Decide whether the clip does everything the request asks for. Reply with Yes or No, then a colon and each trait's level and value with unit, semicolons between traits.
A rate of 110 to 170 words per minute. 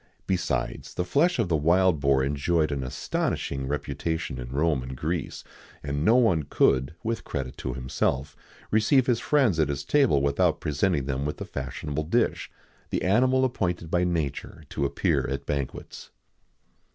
Yes: average, 165 wpm